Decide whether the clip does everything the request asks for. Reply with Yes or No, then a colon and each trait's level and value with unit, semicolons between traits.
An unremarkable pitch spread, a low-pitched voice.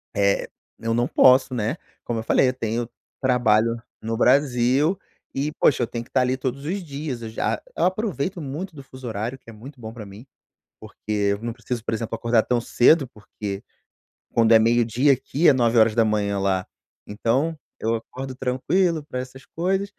Yes: average, 3.4 semitones; low, 125 Hz